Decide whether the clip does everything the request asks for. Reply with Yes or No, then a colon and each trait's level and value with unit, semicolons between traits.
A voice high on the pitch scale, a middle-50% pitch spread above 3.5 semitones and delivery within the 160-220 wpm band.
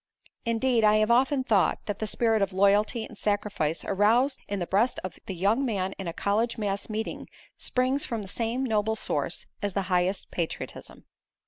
No: high, 210 Hz; average, 2.9 semitones; average, 185 wpm